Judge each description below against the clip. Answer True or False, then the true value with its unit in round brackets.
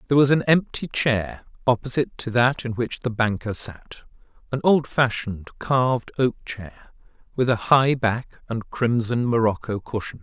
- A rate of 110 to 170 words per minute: True (155 wpm)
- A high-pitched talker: False (120 Hz)